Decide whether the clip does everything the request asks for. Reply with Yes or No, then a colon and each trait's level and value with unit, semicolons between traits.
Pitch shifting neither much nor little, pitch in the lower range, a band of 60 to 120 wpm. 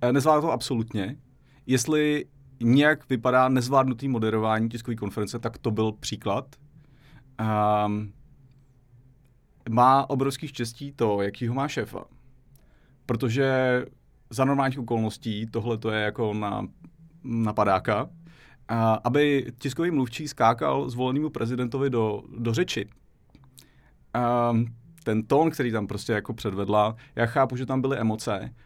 Yes: average, 3.3 semitones; low, 125 Hz; slow, 115 wpm